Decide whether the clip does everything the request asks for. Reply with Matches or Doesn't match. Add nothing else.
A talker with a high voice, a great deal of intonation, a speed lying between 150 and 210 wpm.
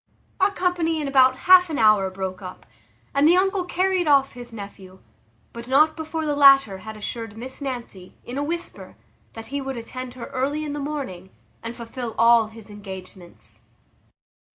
Matches